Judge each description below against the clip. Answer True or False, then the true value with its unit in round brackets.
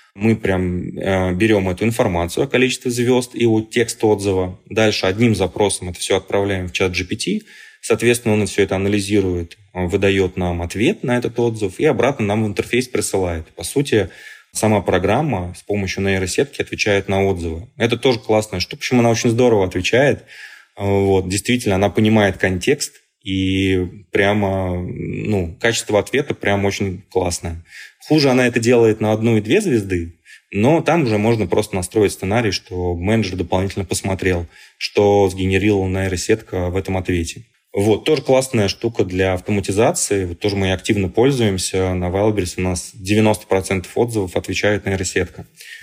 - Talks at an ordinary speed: True (150 wpm)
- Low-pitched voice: True (100 Hz)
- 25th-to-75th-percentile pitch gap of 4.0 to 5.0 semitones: False (3.0 semitones)